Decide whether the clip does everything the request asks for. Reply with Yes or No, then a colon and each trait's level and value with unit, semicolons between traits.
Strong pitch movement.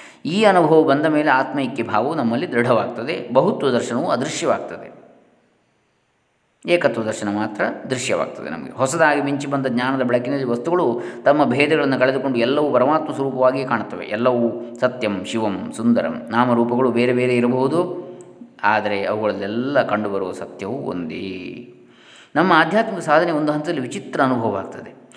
No: average, 4.3 semitones